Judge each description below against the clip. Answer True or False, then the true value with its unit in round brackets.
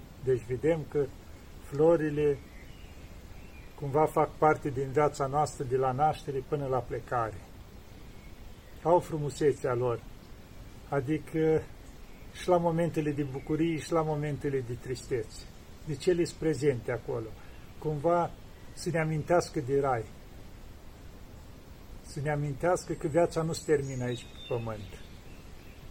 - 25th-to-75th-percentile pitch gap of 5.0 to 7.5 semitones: False (3.8 semitones)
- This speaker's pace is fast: False (125 wpm)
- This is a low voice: False (145 Hz)